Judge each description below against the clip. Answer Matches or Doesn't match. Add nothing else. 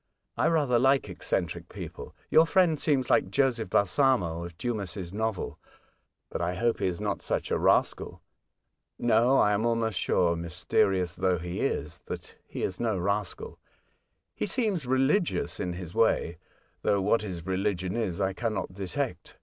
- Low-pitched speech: Matches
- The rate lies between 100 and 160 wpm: Doesn't match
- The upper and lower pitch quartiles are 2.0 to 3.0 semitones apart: Doesn't match